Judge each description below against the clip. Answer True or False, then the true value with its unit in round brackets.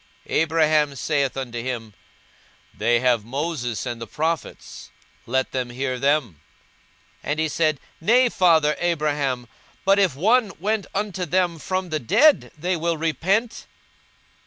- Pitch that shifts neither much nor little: False (5.7 semitones)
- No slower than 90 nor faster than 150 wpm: True (140 wpm)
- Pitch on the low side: False (155 Hz)